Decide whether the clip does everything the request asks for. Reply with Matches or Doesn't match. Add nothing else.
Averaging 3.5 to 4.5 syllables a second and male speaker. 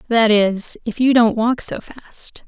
Doesn't match